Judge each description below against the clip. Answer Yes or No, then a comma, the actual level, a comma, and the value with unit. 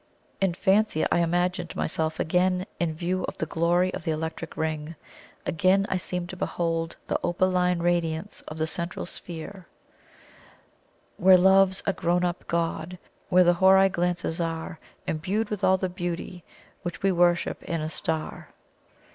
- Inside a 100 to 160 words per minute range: Yes, average, 155 wpm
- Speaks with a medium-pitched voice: Yes, medium, 175 Hz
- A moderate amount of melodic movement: No, narrow, 2.1 semitones